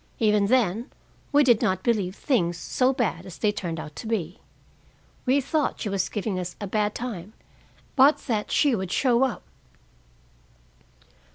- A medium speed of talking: Yes, average, 160 wpm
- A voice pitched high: Yes, high, 210 Hz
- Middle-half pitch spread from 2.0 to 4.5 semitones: No, average, 5.1 semitones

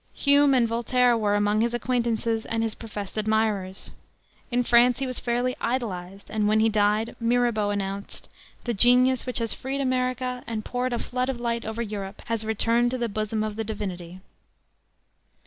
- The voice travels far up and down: No, average, 2.7 semitones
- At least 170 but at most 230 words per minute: Yes, average, 175 wpm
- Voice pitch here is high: Yes, high, 230 Hz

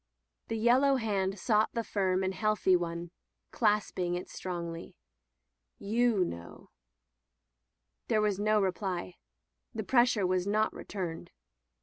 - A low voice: No, high, 195 Hz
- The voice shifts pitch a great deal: No, average, 3.1 semitones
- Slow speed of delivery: Yes, slow, 115 wpm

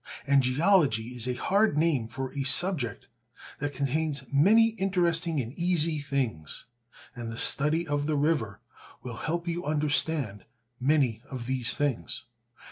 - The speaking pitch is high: No, medium, 145 Hz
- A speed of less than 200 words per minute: Yes, average, 140 wpm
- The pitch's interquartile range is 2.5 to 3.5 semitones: No, average, 4.5 semitones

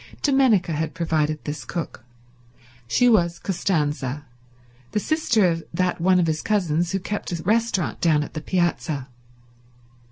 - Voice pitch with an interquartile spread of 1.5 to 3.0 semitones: No, average, 4.1 semitones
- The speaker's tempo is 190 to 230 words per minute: No, average, 140 wpm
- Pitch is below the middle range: No, medium, 170 Hz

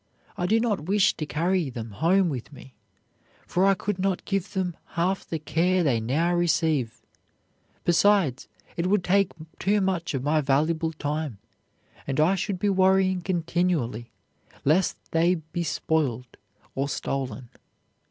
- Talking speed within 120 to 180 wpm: Yes, average, 145 wpm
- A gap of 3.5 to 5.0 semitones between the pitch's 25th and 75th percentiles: Yes, average, 4.6 semitones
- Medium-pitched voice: Yes, medium, 170 Hz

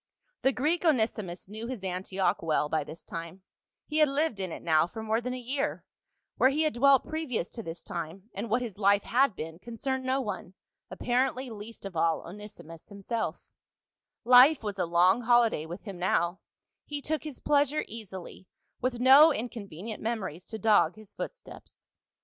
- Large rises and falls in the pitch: Yes, wide, 5.9 semitones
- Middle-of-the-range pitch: No, high, 220 Hz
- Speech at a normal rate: Yes, average, 180 wpm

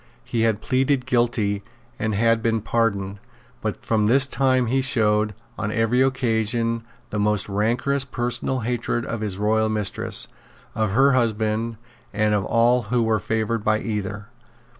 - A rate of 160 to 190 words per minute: No, average, 150 wpm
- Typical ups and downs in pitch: No, narrow, 2.3 semitones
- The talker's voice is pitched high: No, low, 115 Hz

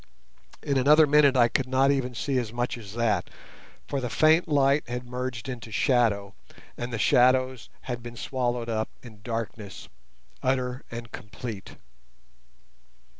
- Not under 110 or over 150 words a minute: Yes, average, 145 wpm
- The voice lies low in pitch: Yes, low, 125 Hz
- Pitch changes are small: Yes, narrow, 2.2 semitones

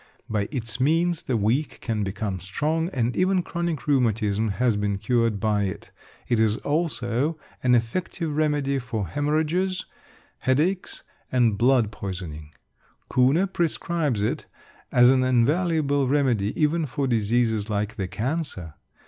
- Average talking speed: No, slow, 130 wpm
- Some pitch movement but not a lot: No, wide, 5.9 semitones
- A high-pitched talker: No, low, 125 Hz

